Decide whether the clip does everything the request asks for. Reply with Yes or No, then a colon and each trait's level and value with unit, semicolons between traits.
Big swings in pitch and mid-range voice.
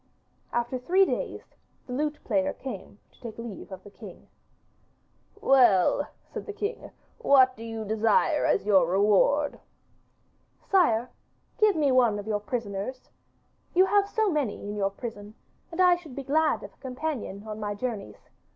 No: wide, 6.4 semitones; very high, 250 Hz